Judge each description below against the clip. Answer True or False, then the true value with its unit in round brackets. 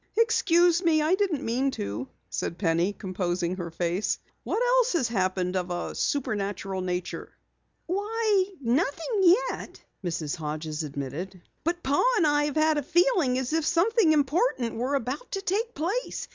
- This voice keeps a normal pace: True (155 wpm)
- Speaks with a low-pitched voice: False (275 Hz)